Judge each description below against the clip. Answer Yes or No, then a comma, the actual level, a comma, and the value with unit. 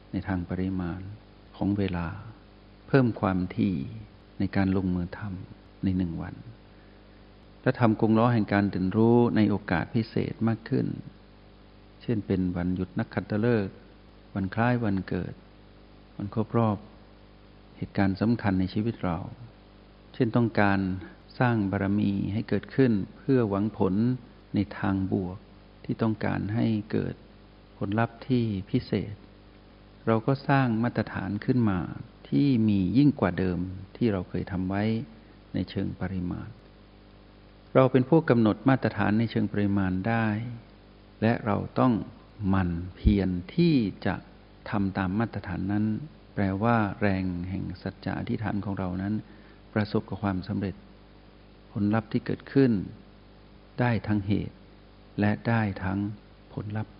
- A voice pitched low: Yes, low, 105 Hz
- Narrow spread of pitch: Yes, narrow, 2.3 semitones